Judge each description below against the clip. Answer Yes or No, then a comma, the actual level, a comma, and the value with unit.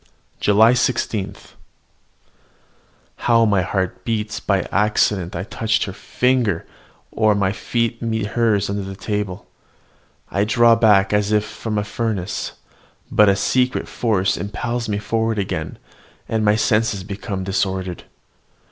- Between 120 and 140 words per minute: Yes, slow, 135 wpm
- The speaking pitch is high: No, low, 105 Hz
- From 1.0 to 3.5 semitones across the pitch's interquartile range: Yes, narrow, 2.5 semitones